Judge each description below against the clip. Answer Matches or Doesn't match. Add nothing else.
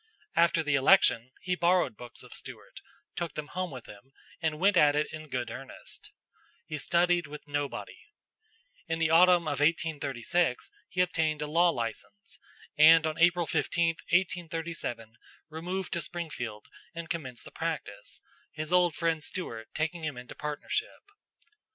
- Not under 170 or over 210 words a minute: Doesn't match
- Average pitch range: Matches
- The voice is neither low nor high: Matches